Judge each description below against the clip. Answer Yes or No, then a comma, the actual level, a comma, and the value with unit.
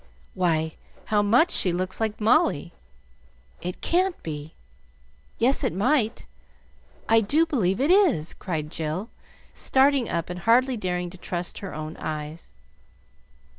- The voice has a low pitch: No, high, 190 Hz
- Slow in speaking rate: Yes, slow, 130 wpm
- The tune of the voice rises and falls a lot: Yes, wide, 7.1 semitones